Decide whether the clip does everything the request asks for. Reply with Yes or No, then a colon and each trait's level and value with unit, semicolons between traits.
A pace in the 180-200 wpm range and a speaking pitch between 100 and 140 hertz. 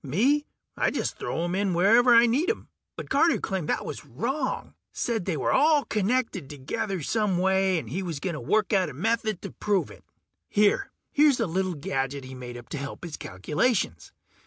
No: average, 195 wpm; high, 190 Hz